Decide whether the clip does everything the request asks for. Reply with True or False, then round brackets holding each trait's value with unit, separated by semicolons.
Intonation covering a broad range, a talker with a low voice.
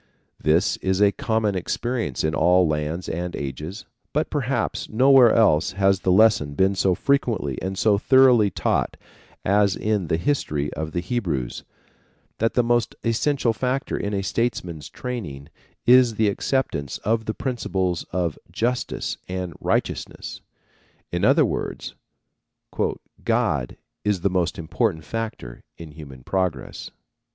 True (5.7 semitones; 95 Hz)